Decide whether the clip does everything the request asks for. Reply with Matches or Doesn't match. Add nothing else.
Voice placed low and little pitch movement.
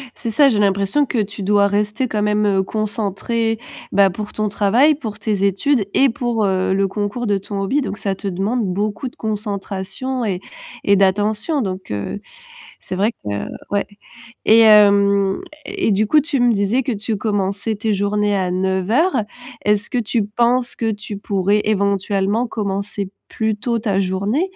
Doesn't match